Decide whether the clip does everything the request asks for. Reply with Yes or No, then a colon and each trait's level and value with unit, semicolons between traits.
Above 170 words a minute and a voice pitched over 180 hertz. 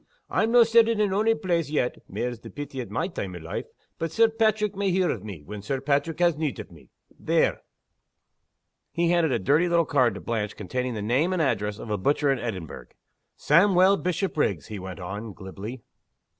No: average, 200 wpm; medium, 140 Hz